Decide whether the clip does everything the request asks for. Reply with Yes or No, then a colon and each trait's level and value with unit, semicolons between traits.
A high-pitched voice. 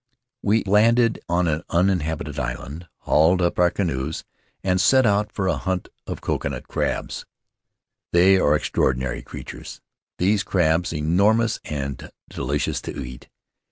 No: very low, 85 Hz